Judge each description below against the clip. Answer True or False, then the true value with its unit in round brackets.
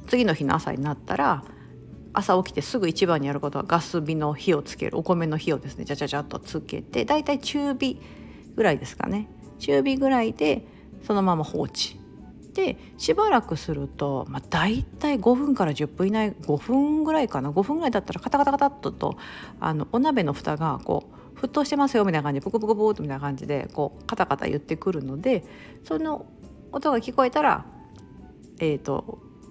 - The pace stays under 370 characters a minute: False (375 characters per minute)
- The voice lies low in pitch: False (190 Hz)